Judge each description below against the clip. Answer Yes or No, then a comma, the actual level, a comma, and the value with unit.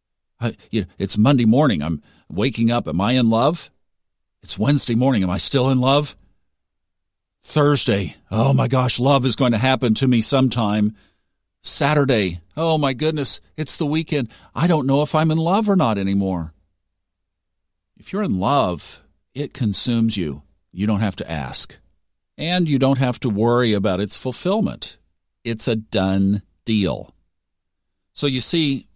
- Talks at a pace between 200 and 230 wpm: No, average, 160 wpm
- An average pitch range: No, wide, 6.8 semitones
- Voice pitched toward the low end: Yes, low, 110 Hz